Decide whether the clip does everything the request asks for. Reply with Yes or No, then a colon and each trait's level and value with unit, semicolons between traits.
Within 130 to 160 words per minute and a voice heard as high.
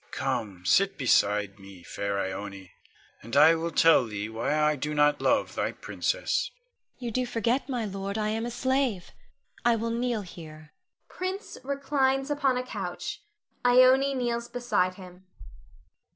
Yes: average, 150 wpm; high, 200 Hz